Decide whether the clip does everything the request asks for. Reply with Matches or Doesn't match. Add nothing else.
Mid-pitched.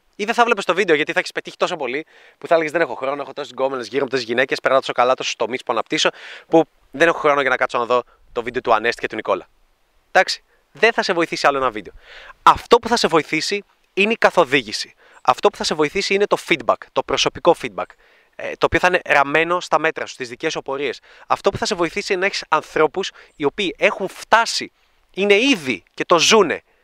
Matches